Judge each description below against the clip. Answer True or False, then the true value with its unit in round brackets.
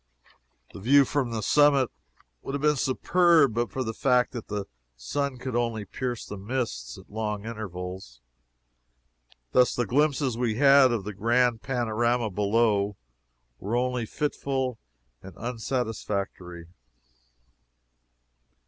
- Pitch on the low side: True (120 Hz)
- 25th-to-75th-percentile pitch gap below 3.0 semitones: False (3.8 semitones)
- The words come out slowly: True (125 wpm)